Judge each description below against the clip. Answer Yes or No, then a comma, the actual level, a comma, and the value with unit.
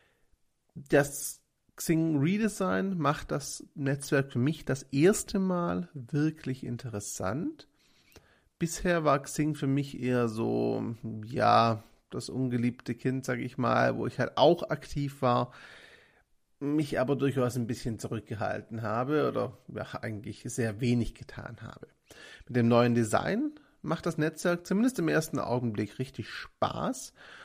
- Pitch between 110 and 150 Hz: Yes, low, 135 Hz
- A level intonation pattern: No, average, 4.5 semitones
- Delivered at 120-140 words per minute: Yes, average, 130 wpm